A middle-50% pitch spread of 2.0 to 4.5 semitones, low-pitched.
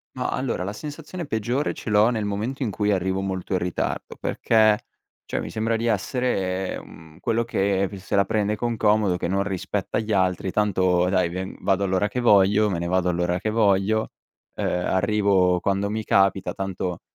Yes: average, 2.7 semitones; low, 100 Hz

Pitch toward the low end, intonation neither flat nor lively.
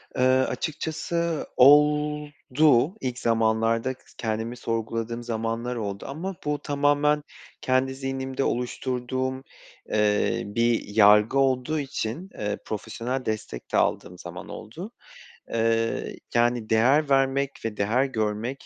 Yes: low, 125 Hz; average, 3.6 semitones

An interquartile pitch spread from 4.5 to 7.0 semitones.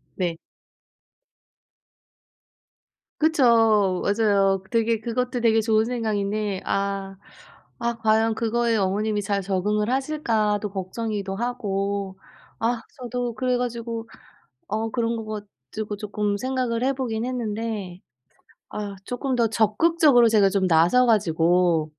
No: average, 3.0 semitones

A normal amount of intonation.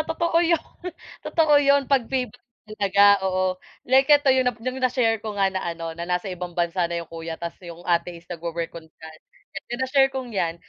No: wide, 7.4 semitones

